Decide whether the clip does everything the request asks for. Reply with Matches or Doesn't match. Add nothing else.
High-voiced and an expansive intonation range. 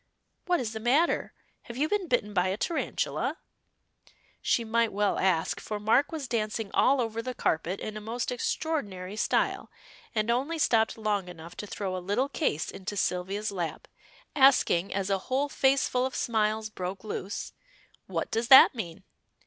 Doesn't match